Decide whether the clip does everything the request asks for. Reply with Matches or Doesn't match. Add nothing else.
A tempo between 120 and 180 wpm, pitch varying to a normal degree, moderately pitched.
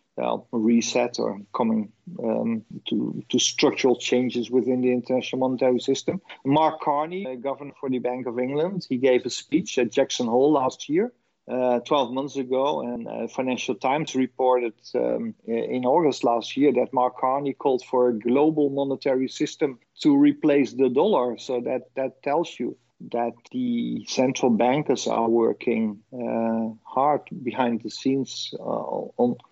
Doesn't match